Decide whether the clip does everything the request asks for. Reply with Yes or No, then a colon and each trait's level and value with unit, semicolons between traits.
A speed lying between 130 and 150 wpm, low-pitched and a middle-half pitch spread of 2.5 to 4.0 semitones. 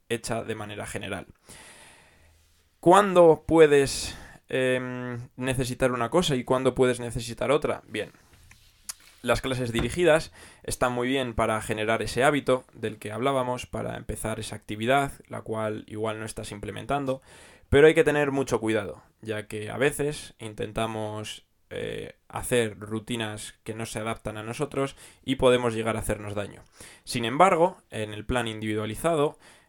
Yes: average, 145 wpm; low, 115 Hz; average, 3.4 semitones